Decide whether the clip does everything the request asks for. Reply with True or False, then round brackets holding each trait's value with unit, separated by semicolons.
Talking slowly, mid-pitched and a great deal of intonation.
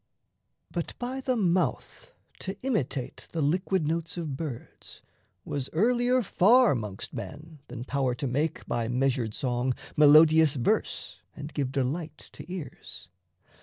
True (130 wpm; 155 Hz; 5.8 semitones)